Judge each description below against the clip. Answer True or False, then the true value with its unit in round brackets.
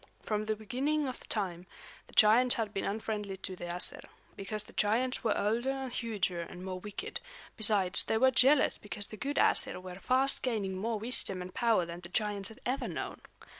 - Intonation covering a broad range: False (4.2 semitones)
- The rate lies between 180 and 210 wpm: True (195 wpm)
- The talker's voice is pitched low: False (215 Hz)